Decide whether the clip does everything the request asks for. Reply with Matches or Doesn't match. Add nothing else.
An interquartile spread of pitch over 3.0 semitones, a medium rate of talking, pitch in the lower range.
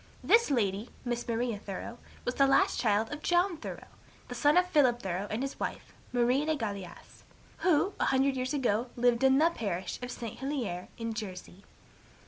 Doesn't match